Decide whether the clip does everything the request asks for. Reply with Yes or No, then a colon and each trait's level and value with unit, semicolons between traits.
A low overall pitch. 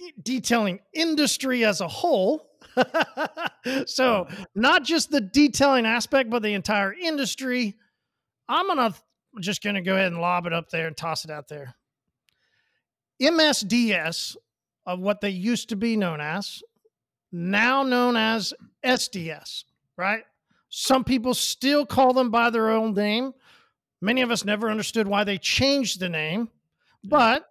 No: high, 225 Hz